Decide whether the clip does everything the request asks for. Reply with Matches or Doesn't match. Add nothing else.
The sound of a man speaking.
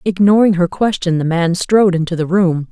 Doesn't match